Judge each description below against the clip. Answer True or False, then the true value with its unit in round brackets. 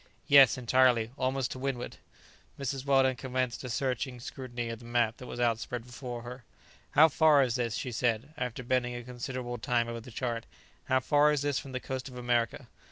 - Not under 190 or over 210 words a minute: True (195 wpm)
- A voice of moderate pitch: False (125 Hz)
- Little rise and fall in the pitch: True (1.7 semitones)